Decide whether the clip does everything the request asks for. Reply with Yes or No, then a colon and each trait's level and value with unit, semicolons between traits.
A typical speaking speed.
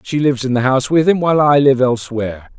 No: fast, 255 wpm